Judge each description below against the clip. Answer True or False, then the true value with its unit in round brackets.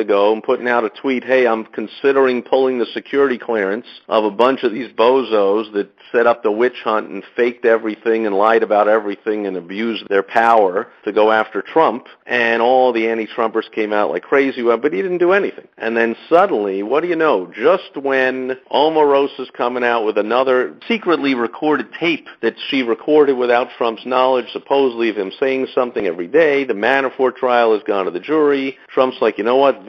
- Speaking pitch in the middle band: False (120 Hz)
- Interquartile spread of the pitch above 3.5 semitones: False (3.1 semitones)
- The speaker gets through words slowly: False (195 wpm)